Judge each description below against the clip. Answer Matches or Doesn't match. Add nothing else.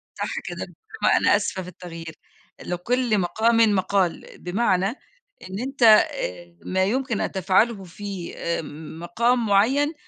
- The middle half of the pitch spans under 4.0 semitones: Doesn't match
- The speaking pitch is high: Matches